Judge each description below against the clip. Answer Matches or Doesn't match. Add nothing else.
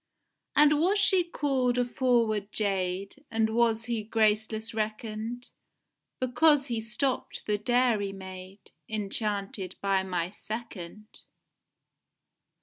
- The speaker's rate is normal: Doesn't match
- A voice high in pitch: Matches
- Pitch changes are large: Doesn't match